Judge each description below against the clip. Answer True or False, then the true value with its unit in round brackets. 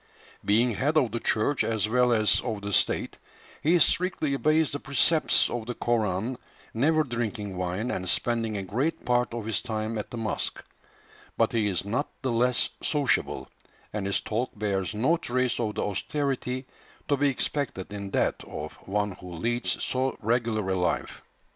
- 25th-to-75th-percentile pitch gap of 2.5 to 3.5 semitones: False (3.9 semitones)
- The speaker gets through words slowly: False (175 wpm)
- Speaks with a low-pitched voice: True (115 Hz)